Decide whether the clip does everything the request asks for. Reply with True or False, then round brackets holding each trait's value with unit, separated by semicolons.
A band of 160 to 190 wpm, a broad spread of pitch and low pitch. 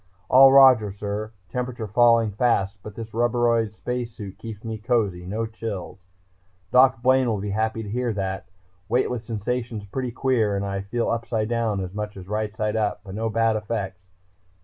False (170 wpm; 2.6 semitones; 110 Hz)